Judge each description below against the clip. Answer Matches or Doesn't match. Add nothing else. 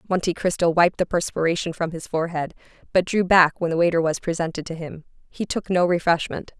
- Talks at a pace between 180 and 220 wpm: Matches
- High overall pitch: Doesn't match